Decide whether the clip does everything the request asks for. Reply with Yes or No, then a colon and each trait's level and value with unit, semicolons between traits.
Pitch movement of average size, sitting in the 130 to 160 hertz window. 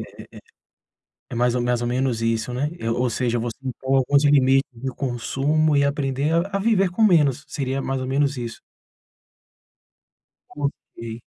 Yes: average, 3.0 semitones; low, 135 Hz